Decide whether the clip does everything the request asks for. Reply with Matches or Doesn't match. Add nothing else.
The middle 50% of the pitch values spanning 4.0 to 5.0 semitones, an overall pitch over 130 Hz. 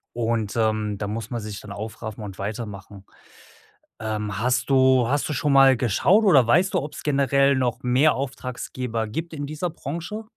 Doesn't match